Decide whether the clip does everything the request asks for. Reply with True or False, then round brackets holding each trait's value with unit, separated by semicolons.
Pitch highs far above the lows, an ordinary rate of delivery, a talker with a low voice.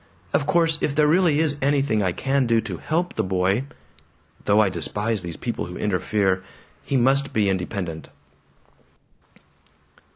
True (7.0 semitones; 150 wpm; 110 Hz)